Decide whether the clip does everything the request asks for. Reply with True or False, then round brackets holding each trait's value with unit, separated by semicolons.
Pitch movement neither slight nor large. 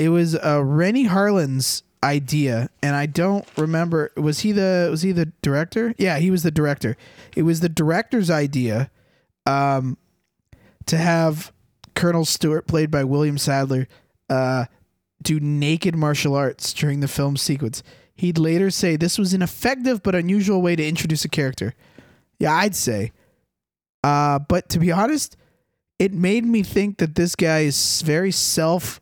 True (4.2 semitones)